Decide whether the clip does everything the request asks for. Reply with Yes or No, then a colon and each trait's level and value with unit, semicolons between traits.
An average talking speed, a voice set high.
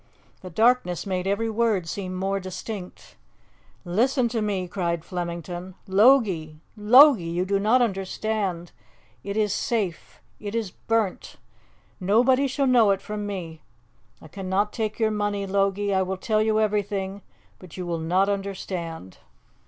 Yes: average, 145 wpm; high, 200 Hz